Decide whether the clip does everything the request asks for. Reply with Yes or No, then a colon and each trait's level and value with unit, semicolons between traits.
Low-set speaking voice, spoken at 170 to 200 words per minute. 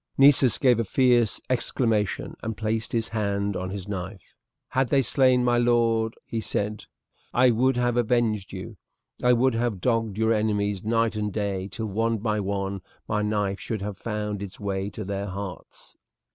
Yes: low, 110 Hz; average, 175 wpm